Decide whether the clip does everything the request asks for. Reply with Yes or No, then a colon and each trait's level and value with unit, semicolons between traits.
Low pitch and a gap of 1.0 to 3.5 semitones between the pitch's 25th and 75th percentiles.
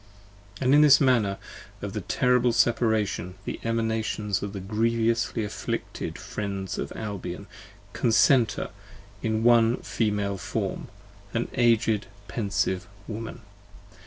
Yes: low, 110 Hz; narrow, 2.5 semitones